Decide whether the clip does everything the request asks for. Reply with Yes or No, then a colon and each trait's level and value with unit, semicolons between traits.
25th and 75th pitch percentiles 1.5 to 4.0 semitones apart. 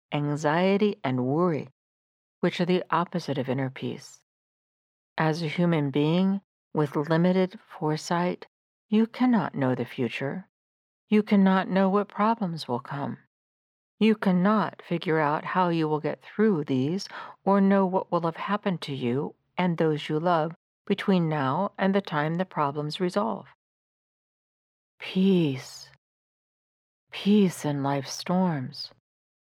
No: average, 4.8 semitones